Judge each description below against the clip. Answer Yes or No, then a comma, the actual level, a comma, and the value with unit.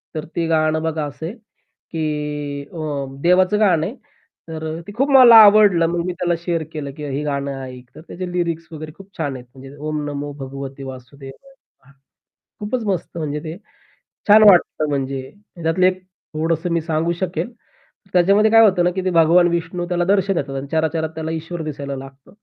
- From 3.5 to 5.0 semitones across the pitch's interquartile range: Yes, average, 3.9 semitones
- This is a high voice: No, medium, 165 Hz